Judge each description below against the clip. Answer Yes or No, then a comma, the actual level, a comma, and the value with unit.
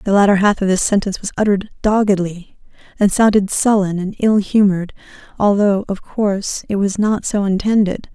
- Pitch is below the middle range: No, high, 200 Hz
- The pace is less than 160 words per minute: No, average, 170 wpm